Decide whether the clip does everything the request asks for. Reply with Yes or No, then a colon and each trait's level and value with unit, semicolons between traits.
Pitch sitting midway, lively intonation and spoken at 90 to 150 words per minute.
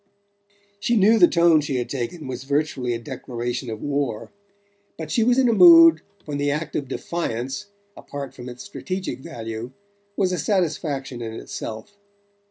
No: medium, 145 Hz; wide, 6.7 semitones; average, 165 wpm